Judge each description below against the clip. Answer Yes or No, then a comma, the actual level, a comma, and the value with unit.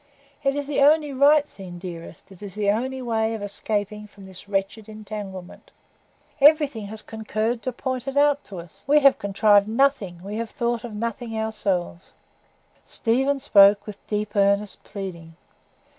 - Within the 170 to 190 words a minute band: No, average, 160 wpm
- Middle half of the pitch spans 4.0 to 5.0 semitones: Yes, average, 4.4 semitones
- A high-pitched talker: Yes, high, 215 Hz